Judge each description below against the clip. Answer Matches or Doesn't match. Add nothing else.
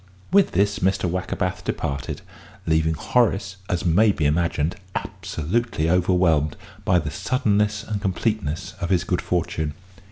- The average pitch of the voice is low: Matches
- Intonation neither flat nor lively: Matches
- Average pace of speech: Doesn't match